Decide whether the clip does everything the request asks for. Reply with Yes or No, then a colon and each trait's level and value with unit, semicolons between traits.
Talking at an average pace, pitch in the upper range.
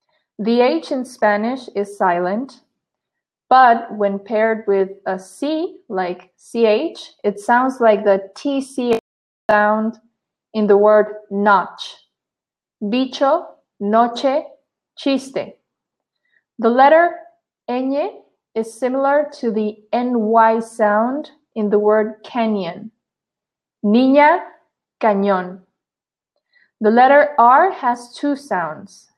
No: slow, 100 wpm; high, 230 Hz